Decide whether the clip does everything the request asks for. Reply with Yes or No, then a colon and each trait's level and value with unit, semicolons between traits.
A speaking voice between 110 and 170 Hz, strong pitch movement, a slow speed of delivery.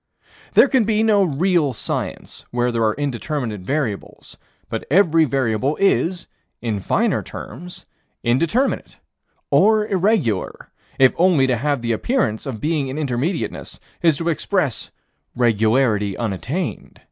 Yes: medium, 140 Hz; wide, 7.1 semitones; slow, 125 wpm